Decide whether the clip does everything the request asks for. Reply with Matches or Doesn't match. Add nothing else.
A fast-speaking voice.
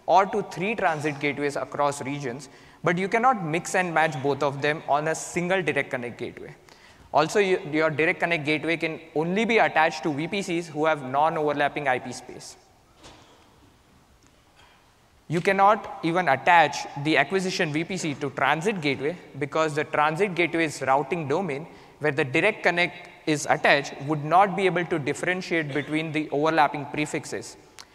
Doesn't match